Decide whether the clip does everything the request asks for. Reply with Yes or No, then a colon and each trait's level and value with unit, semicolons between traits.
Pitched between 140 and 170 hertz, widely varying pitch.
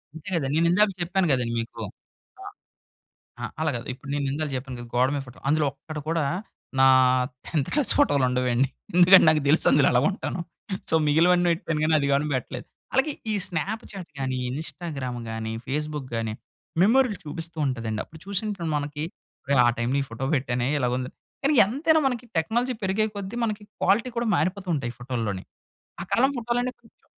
Yes: medium, 155 Hz; wide, 7.2 semitones